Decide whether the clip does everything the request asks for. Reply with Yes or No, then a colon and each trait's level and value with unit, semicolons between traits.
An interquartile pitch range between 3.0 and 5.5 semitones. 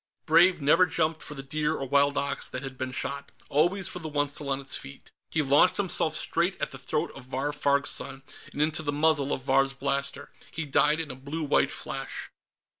No: narrow, 2.5 semitones